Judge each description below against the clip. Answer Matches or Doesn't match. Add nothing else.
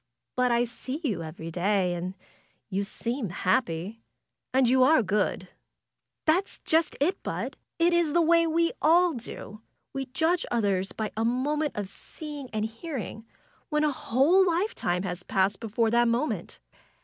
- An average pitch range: Doesn't match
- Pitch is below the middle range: Doesn't match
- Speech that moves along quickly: Doesn't match